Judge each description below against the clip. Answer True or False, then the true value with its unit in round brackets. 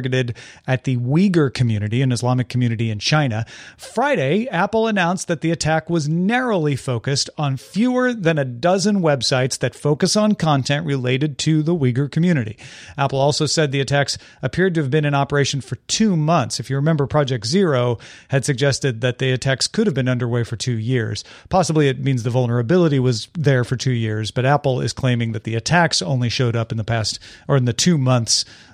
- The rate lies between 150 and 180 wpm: False (190 wpm)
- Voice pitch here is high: False (135 Hz)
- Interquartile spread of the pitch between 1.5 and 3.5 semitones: False (4.2 semitones)